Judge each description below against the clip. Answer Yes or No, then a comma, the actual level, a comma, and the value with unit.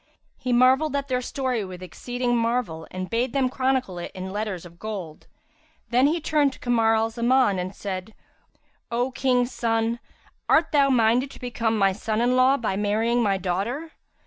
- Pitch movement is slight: No, average, 4.0 semitones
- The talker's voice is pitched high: Yes, high, 235 Hz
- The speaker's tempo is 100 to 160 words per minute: No, average, 175 wpm